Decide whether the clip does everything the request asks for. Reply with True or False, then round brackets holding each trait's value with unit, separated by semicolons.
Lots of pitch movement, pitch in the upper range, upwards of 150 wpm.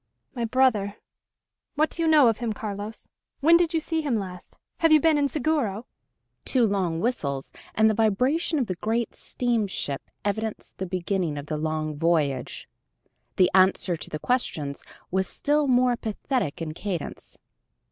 True (6.7 semitones; 215 Hz; 160 wpm)